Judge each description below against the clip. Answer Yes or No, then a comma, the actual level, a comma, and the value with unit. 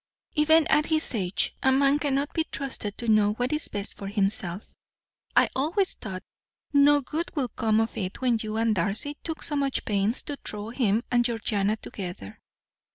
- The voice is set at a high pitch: Yes, high, 235 Hz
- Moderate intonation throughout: No, wide, 5.8 semitones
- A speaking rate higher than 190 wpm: No, average, 180 wpm